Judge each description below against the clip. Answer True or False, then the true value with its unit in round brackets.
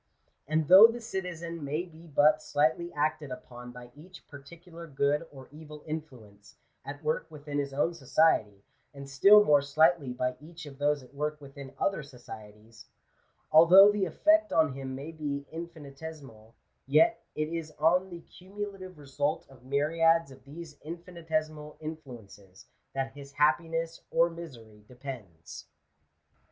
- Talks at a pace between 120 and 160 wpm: True (145 wpm)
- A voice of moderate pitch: True (150 Hz)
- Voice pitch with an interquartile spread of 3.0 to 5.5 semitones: True (3.4 semitones)